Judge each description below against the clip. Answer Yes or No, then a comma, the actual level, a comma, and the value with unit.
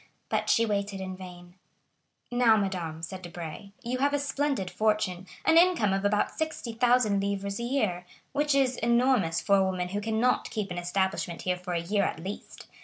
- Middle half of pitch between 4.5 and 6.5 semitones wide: Yes, average, 4.8 semitones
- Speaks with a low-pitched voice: No, high, 200 Hz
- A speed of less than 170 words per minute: No, average, 180 wpm